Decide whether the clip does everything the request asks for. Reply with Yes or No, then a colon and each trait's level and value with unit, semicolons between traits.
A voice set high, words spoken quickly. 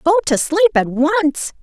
No: very high, 330 Hz; average, 185 wpm